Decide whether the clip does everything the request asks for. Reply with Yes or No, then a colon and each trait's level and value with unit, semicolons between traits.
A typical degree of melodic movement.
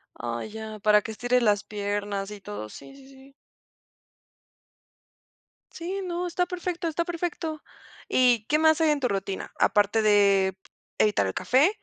No: wide, 7.6 semitones